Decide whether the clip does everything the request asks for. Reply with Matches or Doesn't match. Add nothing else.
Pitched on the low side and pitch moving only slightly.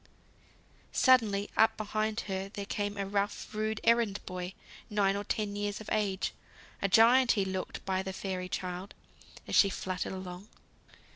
Doesn't match